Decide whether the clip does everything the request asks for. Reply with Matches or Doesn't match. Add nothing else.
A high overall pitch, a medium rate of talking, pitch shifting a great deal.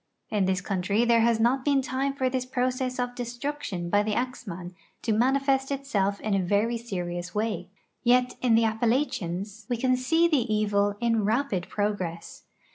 Doesn't match